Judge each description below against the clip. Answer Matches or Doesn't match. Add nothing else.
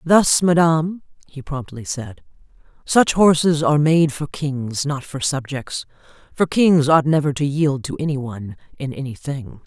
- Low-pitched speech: Doesn't match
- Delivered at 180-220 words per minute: Doesn't match